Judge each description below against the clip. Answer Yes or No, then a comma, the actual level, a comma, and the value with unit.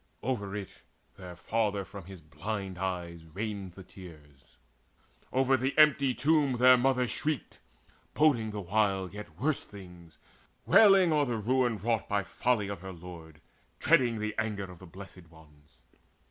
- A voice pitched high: No, low, 100 Hz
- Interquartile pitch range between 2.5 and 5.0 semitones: No, wide, 5.6 semitones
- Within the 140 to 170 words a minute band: Yes, average, 150 wpm